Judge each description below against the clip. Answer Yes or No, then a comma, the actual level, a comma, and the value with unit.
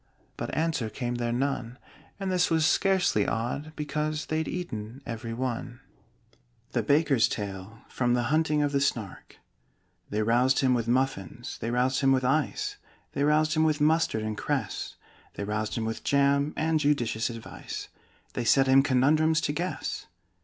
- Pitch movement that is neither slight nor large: Yes, average, 4.7 semitones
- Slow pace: No, average, 160 wpm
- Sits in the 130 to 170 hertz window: Yes, low, 135 Hz